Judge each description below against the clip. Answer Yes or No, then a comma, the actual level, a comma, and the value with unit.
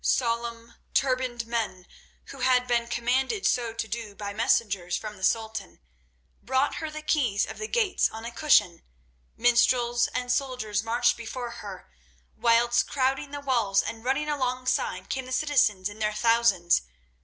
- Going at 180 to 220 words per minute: No, average, 155 wpm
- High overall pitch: Yes, high, 235 Hz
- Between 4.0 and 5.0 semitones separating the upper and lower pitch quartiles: No, average, 2.7 semitones